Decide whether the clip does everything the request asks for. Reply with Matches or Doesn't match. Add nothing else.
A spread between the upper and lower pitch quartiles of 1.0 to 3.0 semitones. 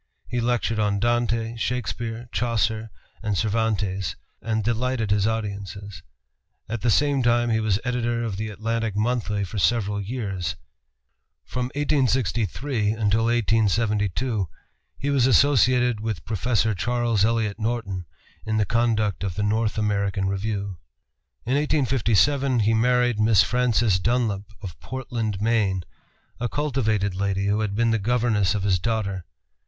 Matches